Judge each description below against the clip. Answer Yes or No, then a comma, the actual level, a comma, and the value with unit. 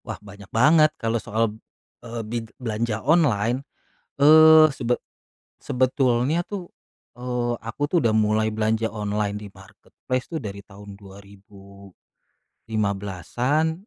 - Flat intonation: No, average, 3.9 semitones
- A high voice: No, low, 115 Hz